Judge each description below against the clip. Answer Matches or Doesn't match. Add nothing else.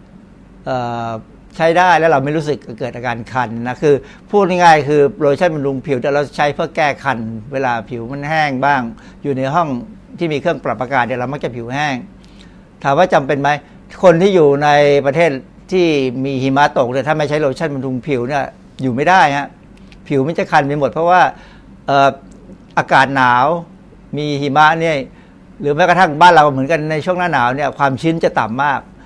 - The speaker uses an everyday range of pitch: Matches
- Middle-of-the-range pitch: Matches